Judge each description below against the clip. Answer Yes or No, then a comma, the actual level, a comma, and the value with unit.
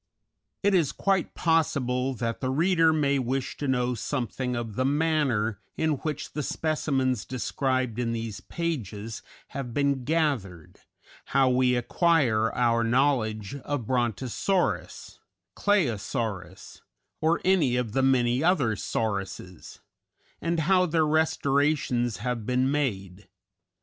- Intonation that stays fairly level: No, average, 4.7 semitones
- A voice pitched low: Yes, low, 130 Hz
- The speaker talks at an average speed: No, slow, 125 wpm